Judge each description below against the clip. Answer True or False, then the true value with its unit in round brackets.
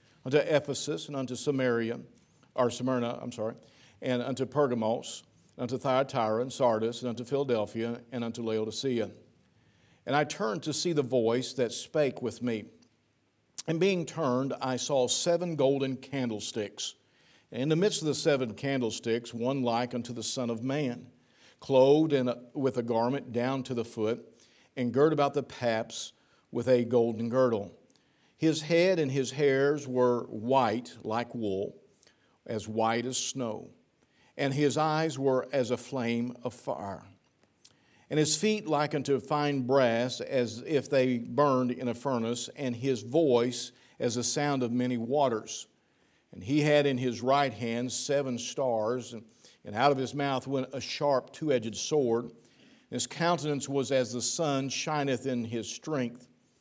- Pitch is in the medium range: False (125 Hz)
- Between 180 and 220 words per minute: False (160 wpm)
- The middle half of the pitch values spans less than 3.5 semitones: True (2.9 semitones)